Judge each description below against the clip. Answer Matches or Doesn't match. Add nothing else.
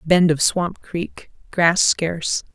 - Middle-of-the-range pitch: Matches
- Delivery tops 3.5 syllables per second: Doesn't match